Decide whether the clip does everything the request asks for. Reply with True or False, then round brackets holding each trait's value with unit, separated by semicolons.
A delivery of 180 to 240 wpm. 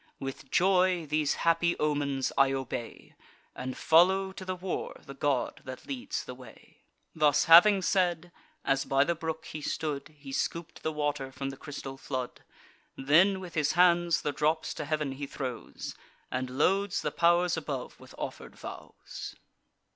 False (160 wpm)